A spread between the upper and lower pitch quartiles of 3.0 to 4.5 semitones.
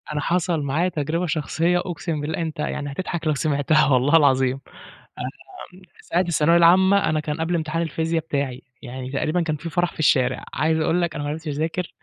No: narrow, 2.6 semitones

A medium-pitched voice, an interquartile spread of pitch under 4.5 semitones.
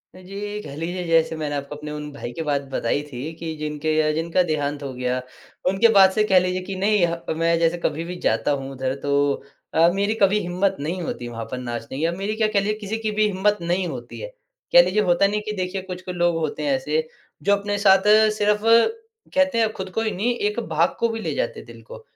No: medium, 175 Hz; average, 5.3 semitones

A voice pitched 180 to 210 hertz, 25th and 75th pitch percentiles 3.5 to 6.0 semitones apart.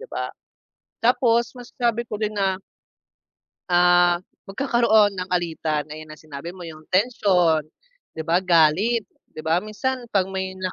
Yes: medium, 185 Hz; average, 4.7 semitones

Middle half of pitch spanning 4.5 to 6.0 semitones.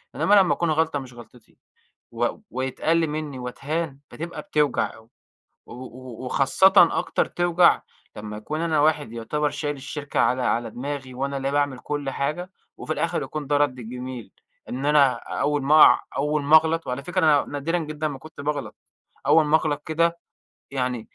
No: average, 3.3 semitones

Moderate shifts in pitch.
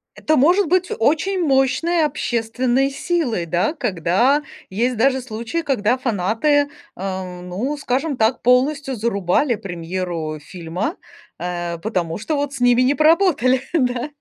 No: wide, 7.3 semitones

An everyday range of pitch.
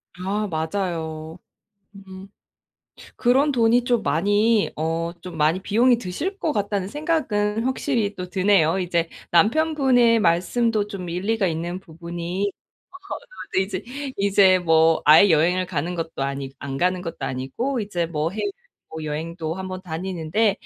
Yes: average, 4.4 semitones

